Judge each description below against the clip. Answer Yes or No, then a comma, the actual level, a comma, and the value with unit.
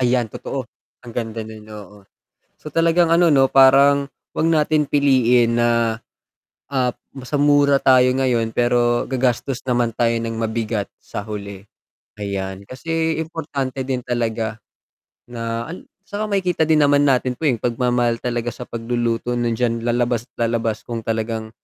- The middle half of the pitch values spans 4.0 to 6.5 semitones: No, average, 3.3 semitones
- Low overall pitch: Yes, low, 120 Hz